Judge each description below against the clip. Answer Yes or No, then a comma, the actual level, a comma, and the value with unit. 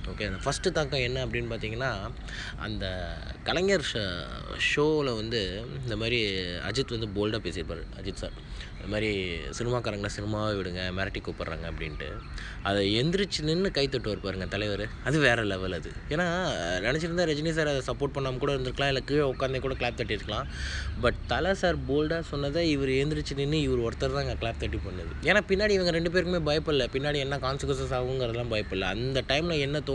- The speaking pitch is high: No, low, 120 Hz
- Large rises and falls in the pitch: Yes, wide, 6.0 semitones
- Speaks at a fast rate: Yes, fast, 165 wpm